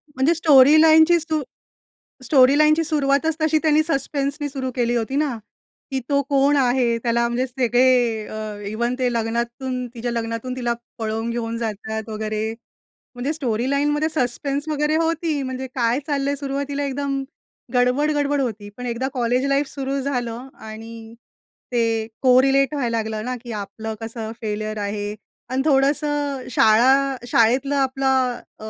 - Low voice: No, very high, 260 Hz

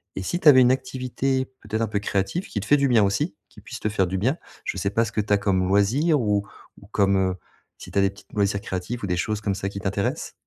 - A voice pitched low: Yes, low, 105 Hz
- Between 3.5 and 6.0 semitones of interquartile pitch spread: Yes, average, 4.2 semitones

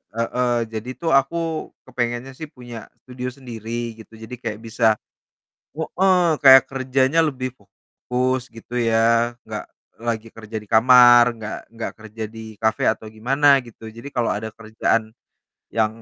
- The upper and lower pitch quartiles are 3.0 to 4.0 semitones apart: No, narrow, 2.6 semitones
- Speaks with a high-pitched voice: No, low, 120 Hz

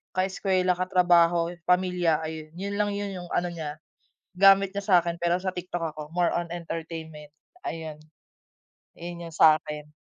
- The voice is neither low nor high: Yes, medium, 175 Hz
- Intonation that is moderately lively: No, narrow, 2.3 semitones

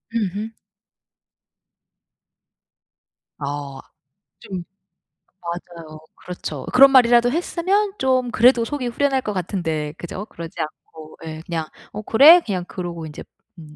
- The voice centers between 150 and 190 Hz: Yes, medium, 185 Hz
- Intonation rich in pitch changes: Yes, wide, 7.6 semitones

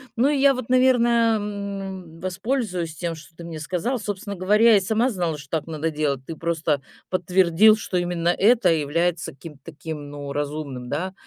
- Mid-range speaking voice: Yes, medium, 175 Hz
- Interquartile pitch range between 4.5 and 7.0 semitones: Yes, average, 5.1 semitones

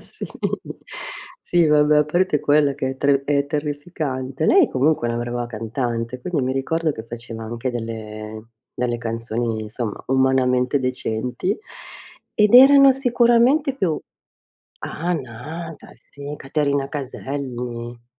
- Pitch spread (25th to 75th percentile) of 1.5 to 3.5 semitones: No, average, 4.5 semitones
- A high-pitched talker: No, low, 135 Hz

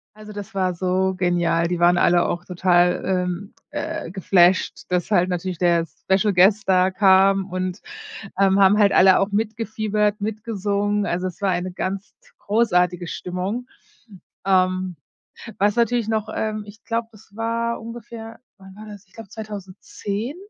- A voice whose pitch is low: No, high, 195 Hz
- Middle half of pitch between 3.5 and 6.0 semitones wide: No, average, 2.8 semitones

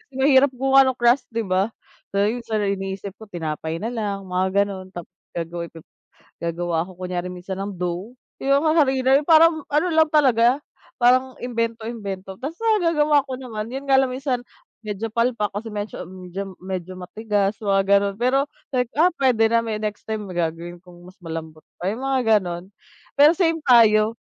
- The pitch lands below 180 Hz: No, high, 220 Hz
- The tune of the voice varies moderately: No, wide, 5.9 semitones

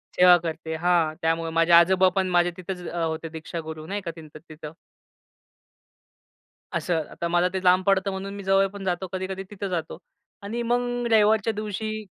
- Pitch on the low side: No, medium, 185 Hz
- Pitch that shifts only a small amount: No, average, 3.1 semitones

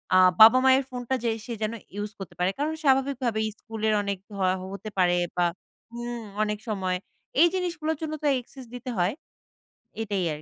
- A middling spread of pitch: Yes, average, 4.8 semitones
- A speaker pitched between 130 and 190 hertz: No, high, 230 Hz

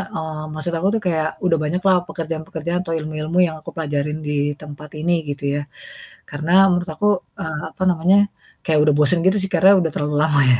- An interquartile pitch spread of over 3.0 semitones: No, narrow, 2.4 semitones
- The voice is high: No, medium, 160 Hz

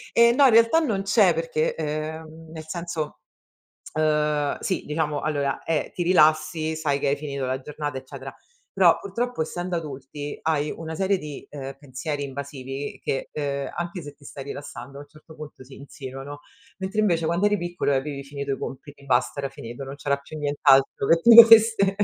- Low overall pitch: No, medium, 150 Hz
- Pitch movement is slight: No, average, 3.2 semitones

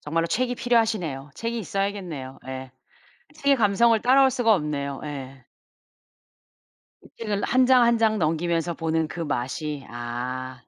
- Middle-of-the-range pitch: Yes, medium, 170 Hz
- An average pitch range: No, wide, 8.6 semitones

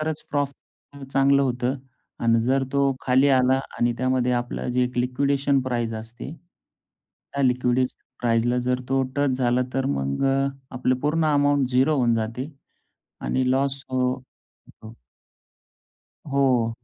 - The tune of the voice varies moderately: No, narrow, 2.0 semitones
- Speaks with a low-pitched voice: Yes, low, 130 Hz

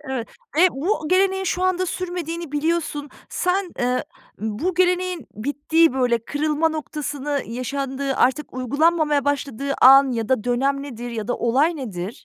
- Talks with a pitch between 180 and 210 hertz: No, very high, 285 Hz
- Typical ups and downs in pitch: Yes, average, 4.7 semitones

